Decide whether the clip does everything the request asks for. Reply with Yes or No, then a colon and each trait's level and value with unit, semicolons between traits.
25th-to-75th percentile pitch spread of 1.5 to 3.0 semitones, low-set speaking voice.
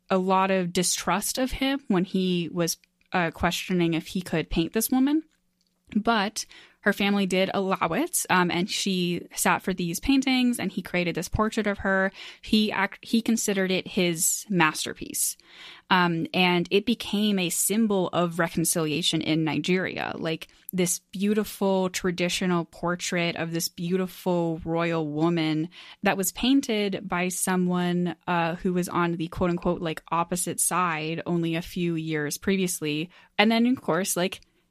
No: average, 2.7 semitones; medium, 180 Hz